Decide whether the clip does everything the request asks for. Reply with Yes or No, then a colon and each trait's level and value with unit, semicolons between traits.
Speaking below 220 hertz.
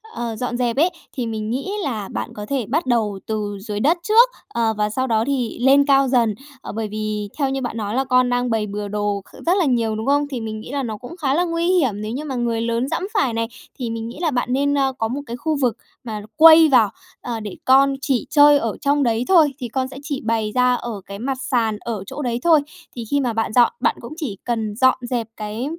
No: high, 245 Hz